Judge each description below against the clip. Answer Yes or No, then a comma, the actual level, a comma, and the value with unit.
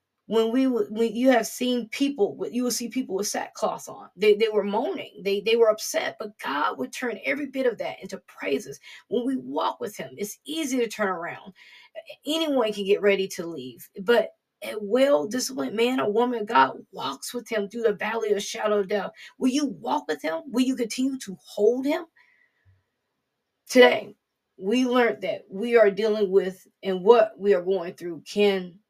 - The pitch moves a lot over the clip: No, average, 4.0 semitones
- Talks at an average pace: Yes, average, 195 wpm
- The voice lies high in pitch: Yes, high, 225 Hz